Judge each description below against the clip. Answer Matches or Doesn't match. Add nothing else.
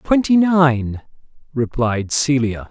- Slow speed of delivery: Matches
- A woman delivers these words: Doesn't match